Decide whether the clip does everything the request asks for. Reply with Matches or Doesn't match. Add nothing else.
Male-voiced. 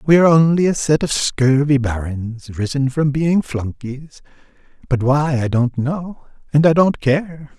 Matches